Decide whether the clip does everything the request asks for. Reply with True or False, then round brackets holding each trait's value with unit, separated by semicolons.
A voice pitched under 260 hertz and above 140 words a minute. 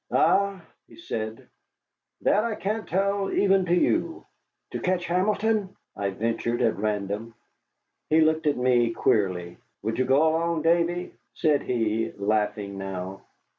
False (140 Hz; 135 wpm)